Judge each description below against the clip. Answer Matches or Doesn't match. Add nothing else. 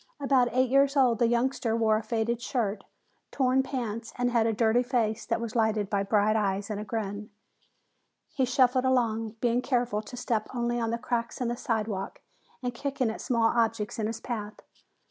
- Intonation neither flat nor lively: Doesn't match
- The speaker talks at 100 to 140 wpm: Doesn't match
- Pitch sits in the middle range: Doesn't match